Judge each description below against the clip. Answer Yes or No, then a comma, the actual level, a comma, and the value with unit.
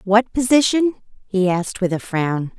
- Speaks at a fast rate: No, average, 160 wpm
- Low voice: No, high, 210 Hz